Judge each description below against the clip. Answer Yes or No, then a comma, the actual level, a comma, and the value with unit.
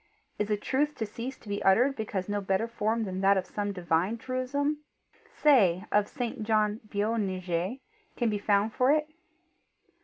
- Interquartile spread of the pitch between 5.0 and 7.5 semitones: No, average, 3.7 semitones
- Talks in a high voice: Yes, high, 210 Hz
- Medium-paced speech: Yes, average, 165 wpm